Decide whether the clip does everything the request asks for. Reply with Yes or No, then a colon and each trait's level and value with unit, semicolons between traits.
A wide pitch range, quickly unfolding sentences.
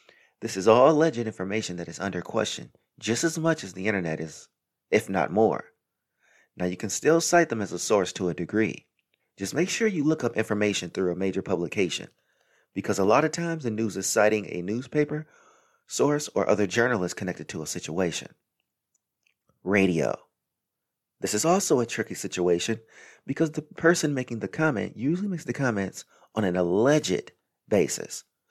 No: wide, 8.7 semitones; average, 175 wpm